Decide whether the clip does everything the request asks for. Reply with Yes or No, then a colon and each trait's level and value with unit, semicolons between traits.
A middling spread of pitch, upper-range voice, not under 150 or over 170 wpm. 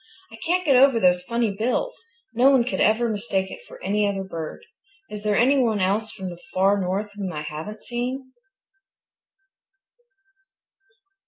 Yes: average, 4.3 semitones; high, 215 Hz; average, 160 wpm